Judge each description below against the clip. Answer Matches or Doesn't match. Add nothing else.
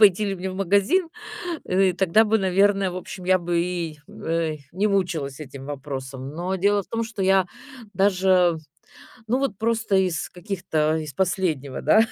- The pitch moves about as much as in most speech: Matches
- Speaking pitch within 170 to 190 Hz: Matches